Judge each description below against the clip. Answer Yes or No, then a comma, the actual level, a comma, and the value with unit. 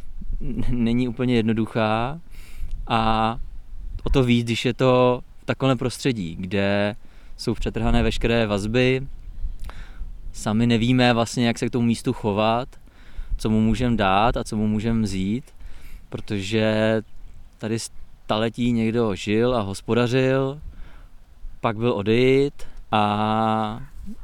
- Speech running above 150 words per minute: No, slow, 115 wpm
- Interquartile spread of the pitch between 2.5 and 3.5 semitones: Yes, average, 3.0 semitones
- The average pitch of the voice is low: Yes, low, 115 Hz